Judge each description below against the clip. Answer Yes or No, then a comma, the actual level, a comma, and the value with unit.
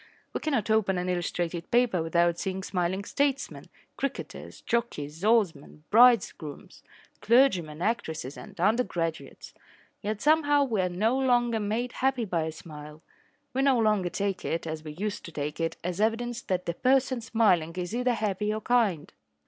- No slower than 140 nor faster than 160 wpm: Yes, average, 155 wpm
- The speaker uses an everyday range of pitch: No, wide, 5.8 semitones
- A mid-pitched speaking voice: No, high, 200 Hz